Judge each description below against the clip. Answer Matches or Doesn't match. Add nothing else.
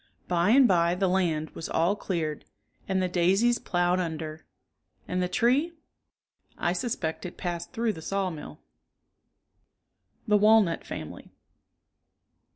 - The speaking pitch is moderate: Matches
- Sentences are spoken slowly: Matches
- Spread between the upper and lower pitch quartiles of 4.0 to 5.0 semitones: Doesn't match